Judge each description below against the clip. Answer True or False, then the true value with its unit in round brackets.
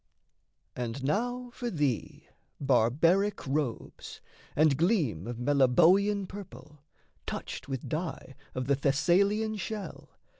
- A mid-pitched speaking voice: True (150 Hz)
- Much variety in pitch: True (7.3 semitones)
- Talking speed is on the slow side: True (105 wpm)